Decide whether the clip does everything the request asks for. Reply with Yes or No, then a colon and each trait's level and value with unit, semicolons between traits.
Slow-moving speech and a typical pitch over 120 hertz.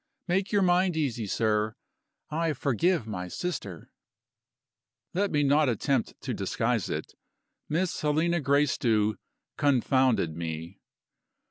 Yes: slow, 110 wpm; medium, 140 Hz